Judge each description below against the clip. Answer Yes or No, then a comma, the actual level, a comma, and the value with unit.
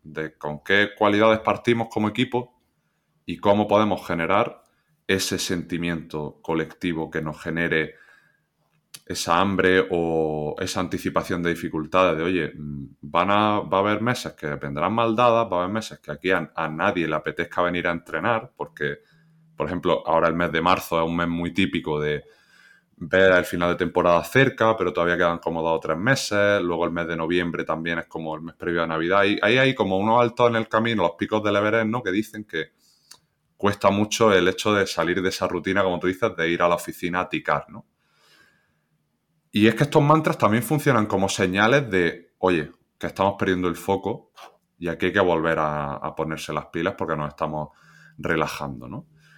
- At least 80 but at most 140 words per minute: No, fast, 190 wpm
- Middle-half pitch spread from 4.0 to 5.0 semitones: Yes, average, 4.6 semitones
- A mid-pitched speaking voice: No, very low, 90 Hz